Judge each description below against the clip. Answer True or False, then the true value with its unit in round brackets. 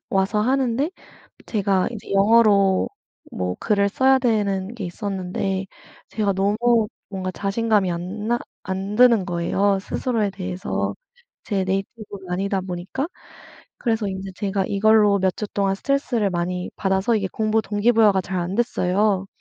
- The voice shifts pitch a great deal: False (2.5 semitones)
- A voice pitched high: True (200 Hz)